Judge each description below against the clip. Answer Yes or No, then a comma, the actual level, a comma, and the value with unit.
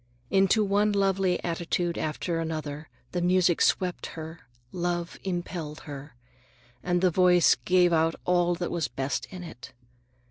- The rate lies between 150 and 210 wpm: No, average, 140 wpm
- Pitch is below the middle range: No, medium, 175 Hz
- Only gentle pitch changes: Yes, narrow, 2.0 semitones